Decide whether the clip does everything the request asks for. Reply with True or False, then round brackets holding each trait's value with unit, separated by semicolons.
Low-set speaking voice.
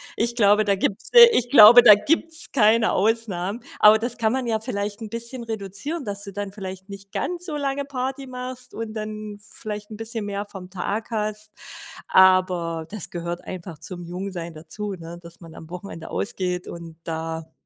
False (205 Hz)